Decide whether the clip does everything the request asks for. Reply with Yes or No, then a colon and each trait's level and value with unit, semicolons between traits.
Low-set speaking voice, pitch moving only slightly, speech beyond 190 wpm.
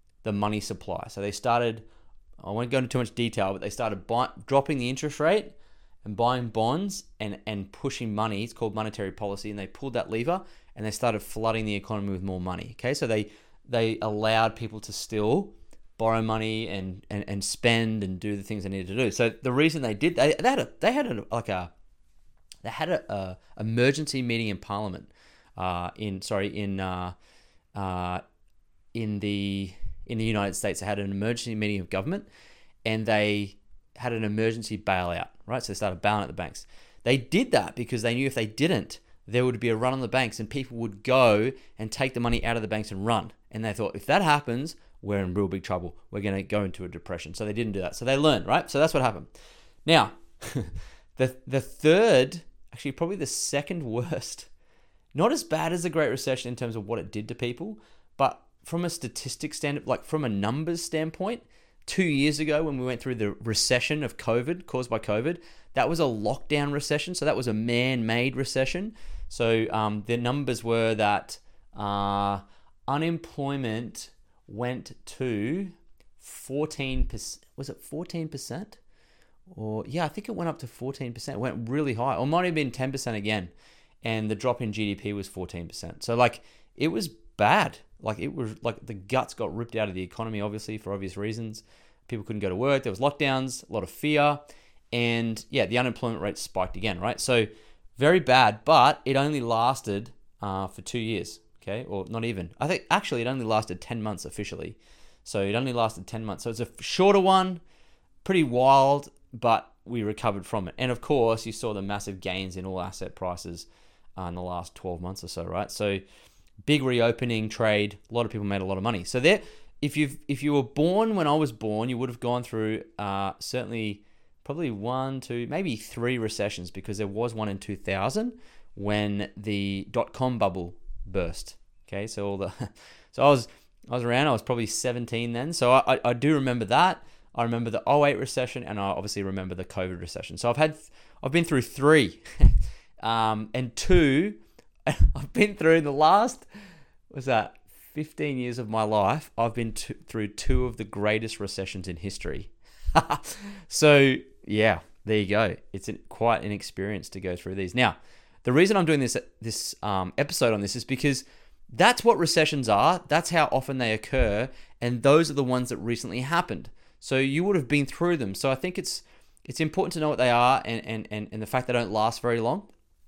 No: low, 115 Hz; average, 4.5 semitones; average, 200 wpm